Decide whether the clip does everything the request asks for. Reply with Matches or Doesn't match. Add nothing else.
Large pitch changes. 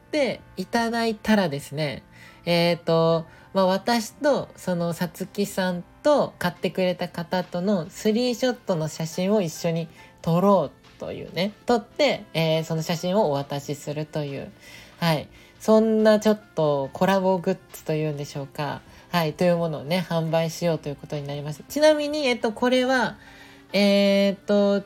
Doesn't match